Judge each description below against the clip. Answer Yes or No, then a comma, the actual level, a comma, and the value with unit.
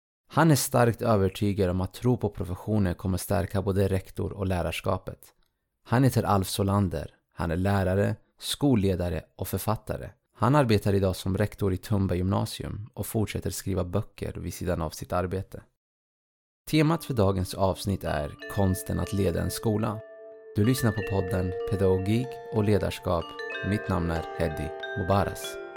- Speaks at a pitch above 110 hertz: No, low, 100 Hz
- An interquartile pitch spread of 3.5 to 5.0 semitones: No, average, 3.0 semitones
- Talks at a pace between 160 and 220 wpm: No, average, 150 wpm